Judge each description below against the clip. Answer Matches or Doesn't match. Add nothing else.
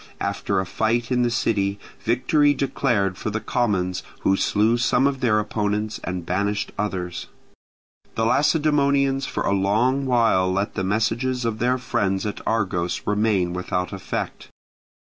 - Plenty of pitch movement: Doesn't match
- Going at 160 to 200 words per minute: Doesn't match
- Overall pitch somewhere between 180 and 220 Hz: Doesn't match